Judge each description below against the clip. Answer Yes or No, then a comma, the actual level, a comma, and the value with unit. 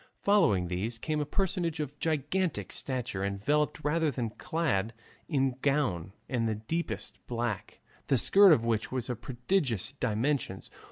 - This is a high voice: No, low, 130 Hz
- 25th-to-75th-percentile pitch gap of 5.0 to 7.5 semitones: Yes, wide, 5.5 semitones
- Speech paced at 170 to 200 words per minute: No, average, 150 wpm